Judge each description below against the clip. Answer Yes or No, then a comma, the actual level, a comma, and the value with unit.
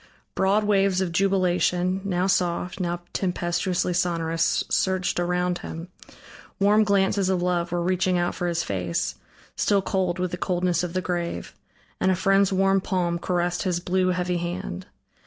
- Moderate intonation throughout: No, narrow, 1.4 semitones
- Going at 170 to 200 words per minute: No, average, 155 wpm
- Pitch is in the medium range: Yes, medium, 180 Hz